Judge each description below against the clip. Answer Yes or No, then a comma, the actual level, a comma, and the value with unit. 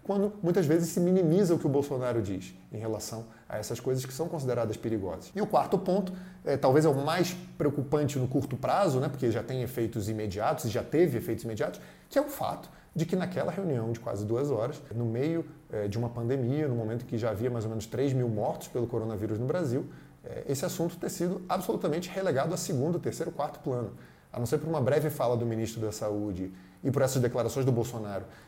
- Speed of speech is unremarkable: No, fast, 225 wpm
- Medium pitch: No, low, 130 Hz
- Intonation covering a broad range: Yes, wide, 6.2 semitones